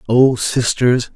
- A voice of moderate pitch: No, low, 120 Hz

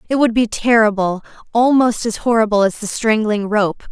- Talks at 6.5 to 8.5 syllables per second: No, 5.1 syllables/s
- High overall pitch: Yes, high, 220 Hz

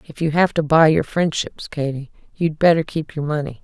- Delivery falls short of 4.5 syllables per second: No, 5.2 syllables/s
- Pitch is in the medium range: Yes, medium, 155 Hz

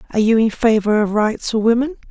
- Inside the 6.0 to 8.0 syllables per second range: Yes, 6.3 syllables/s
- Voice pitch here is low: No, high, 225 Hz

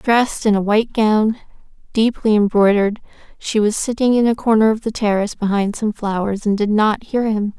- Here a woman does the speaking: Yes, female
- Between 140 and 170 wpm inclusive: No, average, 190 wpm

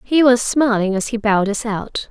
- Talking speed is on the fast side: Yes, fast, 230 wpm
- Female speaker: Yes, female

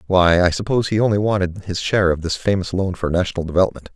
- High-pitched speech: No, very low, 90 Hz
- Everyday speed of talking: No, fast, 230 wpm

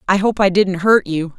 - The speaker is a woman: Yes, female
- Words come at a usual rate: No, fast, 260 wpm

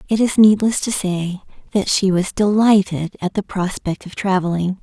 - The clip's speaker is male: No, female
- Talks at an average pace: Yes, average, 175 wpm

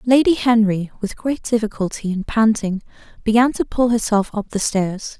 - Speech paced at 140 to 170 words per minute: Yes, average, 160 wpm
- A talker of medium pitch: No, high, 220 Hz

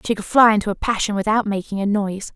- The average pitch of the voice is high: Yes, high, 205 Hz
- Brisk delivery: Yes, fast, 255 wpm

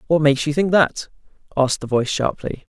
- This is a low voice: No, medium, 145 Hz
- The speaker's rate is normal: Yes, average, 195 wpm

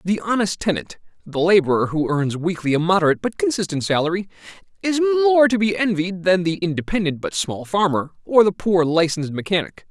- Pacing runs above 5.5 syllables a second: Yes, 5.7 syllables/s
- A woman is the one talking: No, male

